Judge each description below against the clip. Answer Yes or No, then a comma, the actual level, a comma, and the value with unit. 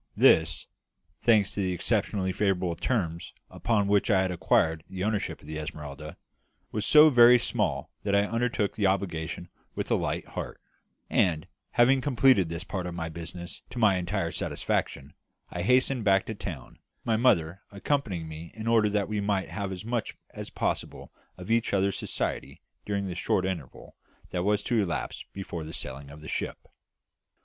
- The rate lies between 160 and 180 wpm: Yes, average, 175 wpm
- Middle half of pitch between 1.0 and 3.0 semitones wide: No, average, 4.3 semitones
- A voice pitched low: Yes, very low, 95 Hz